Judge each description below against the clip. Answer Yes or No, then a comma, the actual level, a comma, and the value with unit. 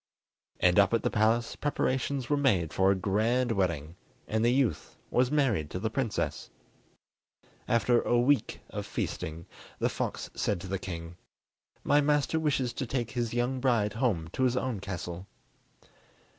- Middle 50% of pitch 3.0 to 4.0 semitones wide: No, average, 5.2 semitones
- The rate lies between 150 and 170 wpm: Yes, average, 160 wpm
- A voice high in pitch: No, low, 115 Hz